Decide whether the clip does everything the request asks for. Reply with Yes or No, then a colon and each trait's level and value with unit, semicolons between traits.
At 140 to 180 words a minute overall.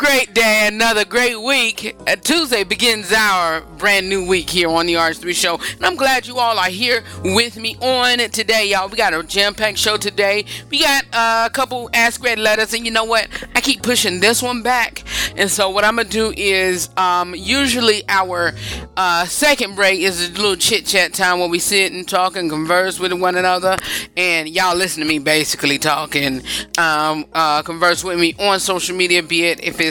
No: fast, 205 wpm